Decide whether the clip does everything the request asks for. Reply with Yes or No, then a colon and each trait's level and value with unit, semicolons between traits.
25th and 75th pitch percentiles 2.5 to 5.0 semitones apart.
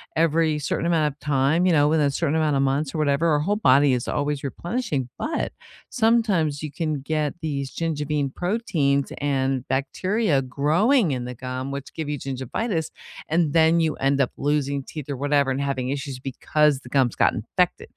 Yes: average, 2.8 semitones